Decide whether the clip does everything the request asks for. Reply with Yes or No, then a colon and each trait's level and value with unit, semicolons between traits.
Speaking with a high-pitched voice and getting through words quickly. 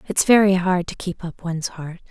No: medium, 180 Hz; fast, 230 wpm